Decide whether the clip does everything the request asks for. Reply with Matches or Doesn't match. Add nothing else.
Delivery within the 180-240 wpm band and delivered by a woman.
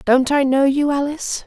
Matches